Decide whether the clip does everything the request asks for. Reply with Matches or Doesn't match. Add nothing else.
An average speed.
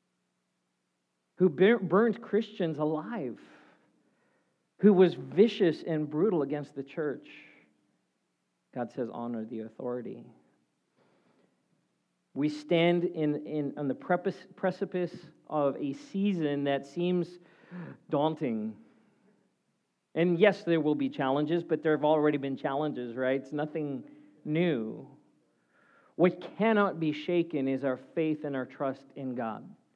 Doesn't match